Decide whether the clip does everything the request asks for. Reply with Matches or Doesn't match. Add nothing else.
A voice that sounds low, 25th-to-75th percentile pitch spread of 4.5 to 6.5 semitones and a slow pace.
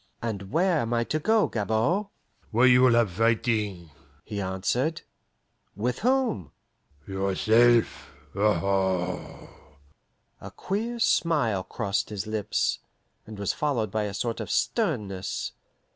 Matches